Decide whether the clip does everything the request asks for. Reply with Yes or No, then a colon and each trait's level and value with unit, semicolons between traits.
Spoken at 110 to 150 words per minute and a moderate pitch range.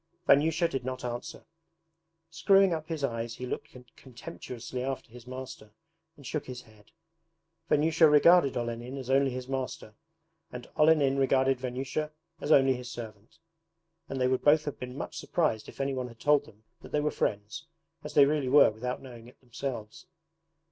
No: average, 170 wpm; average, 3.1 semitones